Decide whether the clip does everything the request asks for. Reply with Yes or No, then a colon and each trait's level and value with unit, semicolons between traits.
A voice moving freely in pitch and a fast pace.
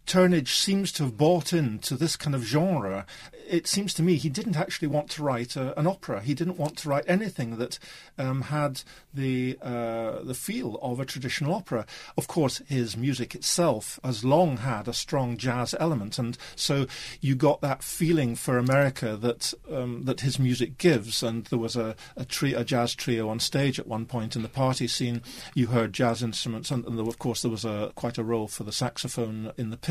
No: average, 3.9 semitones; fast, 210 wpm